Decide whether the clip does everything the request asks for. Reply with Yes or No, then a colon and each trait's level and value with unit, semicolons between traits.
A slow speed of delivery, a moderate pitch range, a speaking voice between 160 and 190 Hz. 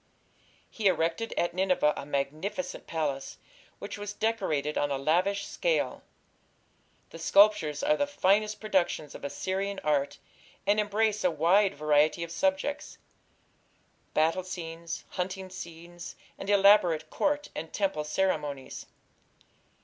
Yes: slow, 120 wpm; average, 4.8 semitones; medium, 185 Hz